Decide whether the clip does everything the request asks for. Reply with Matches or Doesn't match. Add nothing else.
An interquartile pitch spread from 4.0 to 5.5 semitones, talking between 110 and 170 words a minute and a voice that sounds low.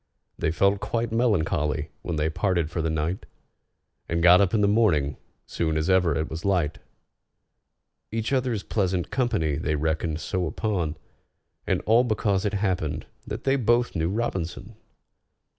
Matches